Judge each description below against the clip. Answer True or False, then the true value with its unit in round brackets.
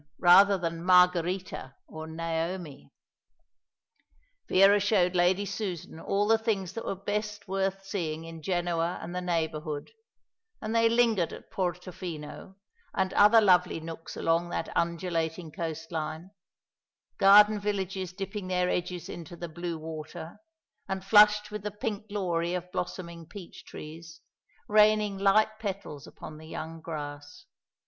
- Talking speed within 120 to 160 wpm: True (135 wpm)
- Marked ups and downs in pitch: False (3.3 semitones)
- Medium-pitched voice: True (180 Hz)